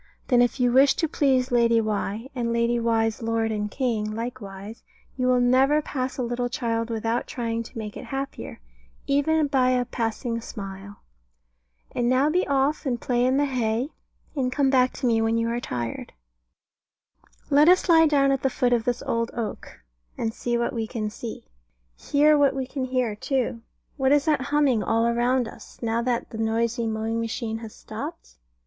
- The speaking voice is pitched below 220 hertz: No, high, 240 Hz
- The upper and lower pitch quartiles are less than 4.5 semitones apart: Yes, average, 2.8 semitones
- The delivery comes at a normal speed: Yes, average, 190 wpm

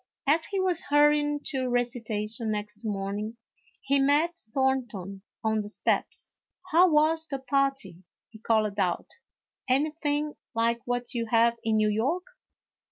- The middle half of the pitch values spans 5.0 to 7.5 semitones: Yes, average, 5.3 semitones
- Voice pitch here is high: Yes, high, 245 Hz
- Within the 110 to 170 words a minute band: Yes, average, 150 wpm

